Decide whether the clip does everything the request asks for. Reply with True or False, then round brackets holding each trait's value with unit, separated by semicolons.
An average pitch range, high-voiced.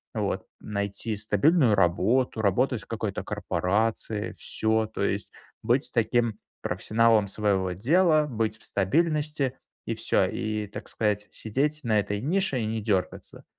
False (3.8 semitones; 110 Hz)